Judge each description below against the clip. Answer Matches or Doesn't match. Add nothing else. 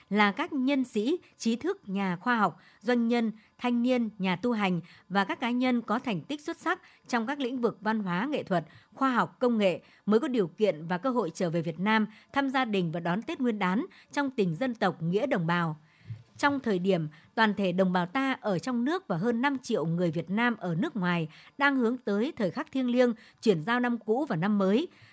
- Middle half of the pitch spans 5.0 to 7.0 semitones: Matches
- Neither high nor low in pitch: Doesn't match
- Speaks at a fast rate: Doesn't match